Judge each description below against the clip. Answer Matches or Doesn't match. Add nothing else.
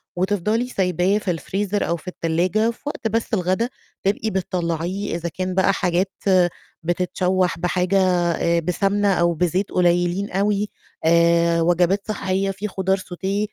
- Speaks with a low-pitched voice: Doesn't match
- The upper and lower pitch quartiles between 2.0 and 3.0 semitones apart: Matches